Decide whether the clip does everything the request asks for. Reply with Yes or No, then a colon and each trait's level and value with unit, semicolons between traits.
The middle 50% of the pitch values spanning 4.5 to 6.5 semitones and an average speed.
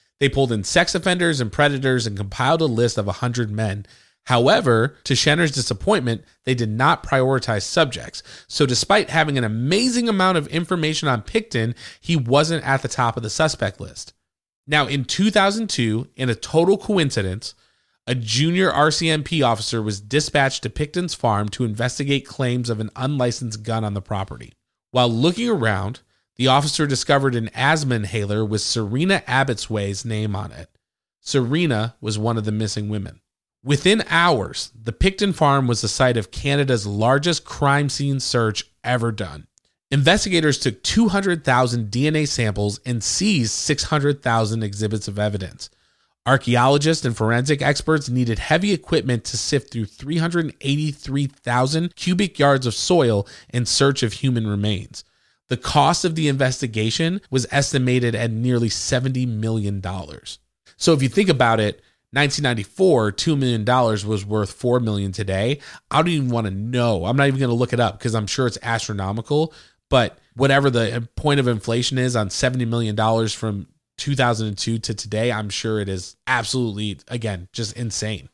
Yes: average, 4.9 semitones; average, 155 wpm